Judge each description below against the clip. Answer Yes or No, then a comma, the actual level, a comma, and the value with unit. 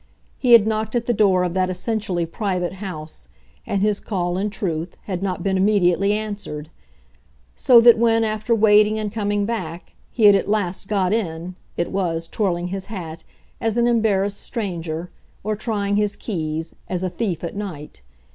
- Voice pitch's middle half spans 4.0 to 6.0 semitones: No, average, 3.4 semitones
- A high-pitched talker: Yes, high, 200 Hz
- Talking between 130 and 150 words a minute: No, average, 175 wpm